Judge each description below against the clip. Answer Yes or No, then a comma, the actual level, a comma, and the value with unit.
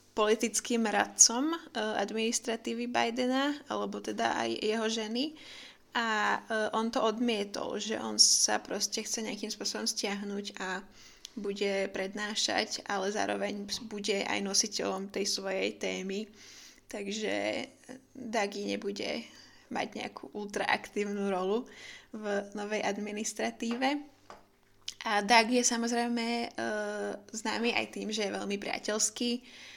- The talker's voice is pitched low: No, high, 215 Hz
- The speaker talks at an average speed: No, slow, 105 wpm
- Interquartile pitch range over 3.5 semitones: No, narrow, 2.5 semitones